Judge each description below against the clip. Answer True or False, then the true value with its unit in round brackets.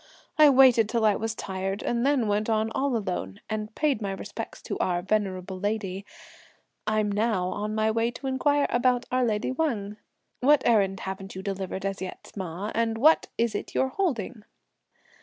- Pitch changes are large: False (3.8 semitones)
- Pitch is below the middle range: False (215 Hz)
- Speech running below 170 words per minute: False (175 wpm)